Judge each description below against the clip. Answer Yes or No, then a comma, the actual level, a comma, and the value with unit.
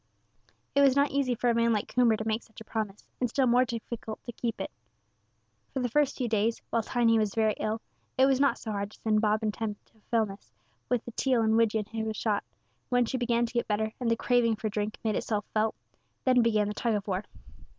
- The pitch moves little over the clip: Yes, narrow, 2.1 semitones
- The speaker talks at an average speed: No, fast, 245 wpm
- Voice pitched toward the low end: No, high, 225 Hz